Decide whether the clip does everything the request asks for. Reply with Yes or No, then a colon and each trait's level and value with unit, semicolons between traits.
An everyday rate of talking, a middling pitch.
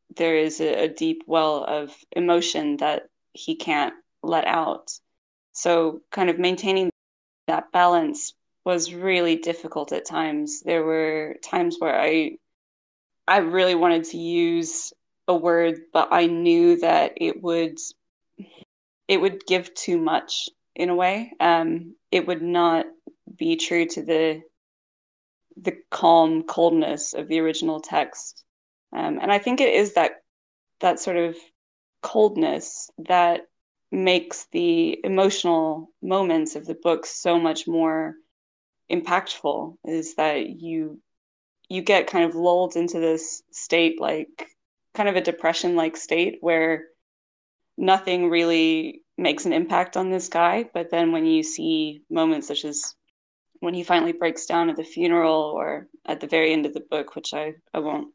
Yes: average, 145 wpm; medium, 175 Hz